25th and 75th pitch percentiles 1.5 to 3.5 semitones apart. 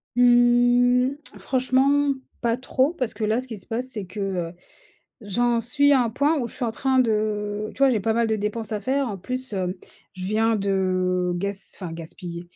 No: average, 4.0 semitones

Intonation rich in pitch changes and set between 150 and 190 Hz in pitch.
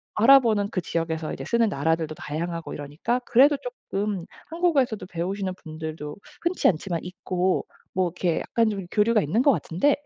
Yes: wide, 5.9 semitones; medium, 185 Hz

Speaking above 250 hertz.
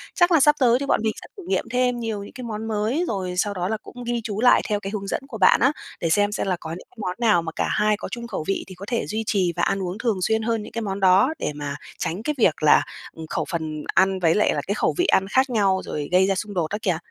No: high, 210 Hz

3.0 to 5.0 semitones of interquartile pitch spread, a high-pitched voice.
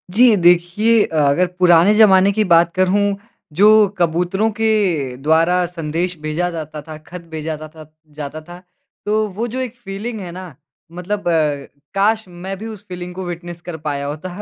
No: average, 3.7 semitones; medium, 180 Hz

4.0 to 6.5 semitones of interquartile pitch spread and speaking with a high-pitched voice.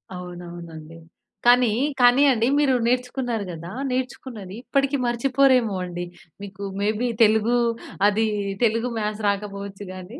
Yes: average, 4.4 semitones; high, 220 Hz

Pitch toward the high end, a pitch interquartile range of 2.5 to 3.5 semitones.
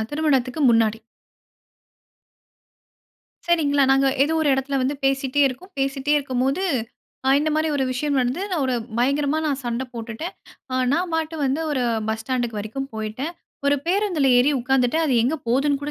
Yes: very high, 275 Hz; average, 3.0 semitones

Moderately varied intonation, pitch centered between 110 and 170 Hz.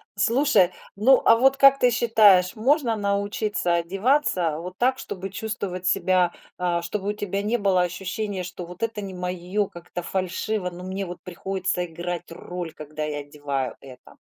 No: average, 3.1 semitones; medium, 185 Hz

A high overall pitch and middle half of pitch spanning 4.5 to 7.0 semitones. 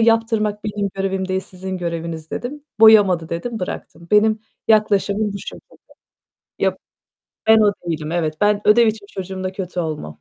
No: high, 200 Hz; average, 3.2 semitones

